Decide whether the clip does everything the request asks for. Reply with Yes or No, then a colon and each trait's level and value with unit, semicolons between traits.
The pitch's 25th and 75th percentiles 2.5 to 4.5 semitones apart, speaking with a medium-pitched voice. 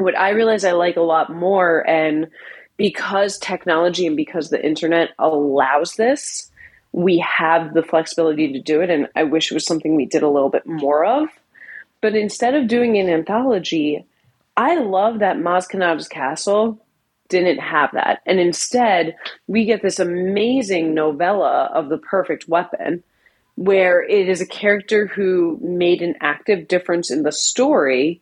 Yes: average, 3.9 semitones; medium, 175 Hz